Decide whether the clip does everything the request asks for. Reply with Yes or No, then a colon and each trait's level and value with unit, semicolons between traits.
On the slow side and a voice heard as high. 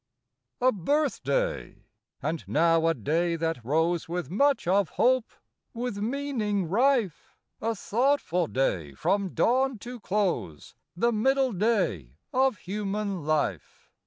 Yes: slow, 125 wpm; high, 200 Hz